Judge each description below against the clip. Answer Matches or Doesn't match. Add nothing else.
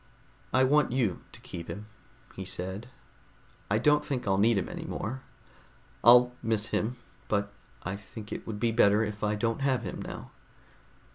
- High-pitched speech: Doesn't match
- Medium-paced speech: Matches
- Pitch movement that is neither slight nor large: Matches